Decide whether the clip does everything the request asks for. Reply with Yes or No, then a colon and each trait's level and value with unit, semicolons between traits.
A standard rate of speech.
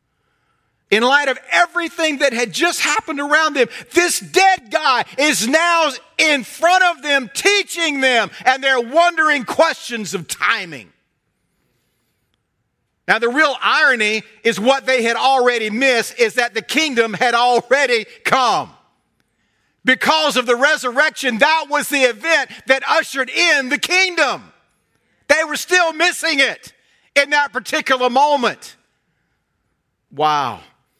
No: slow, 130 wpm